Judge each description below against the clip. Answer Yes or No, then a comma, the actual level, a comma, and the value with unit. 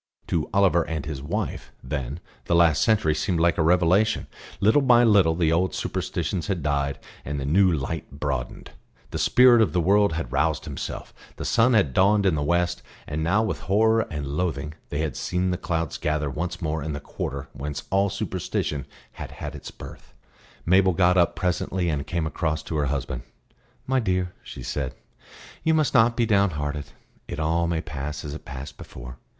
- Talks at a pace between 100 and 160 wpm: No, average, 190 wpm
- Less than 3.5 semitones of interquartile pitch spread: No, average, 4.6 semitones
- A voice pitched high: No, very low, 85 Hz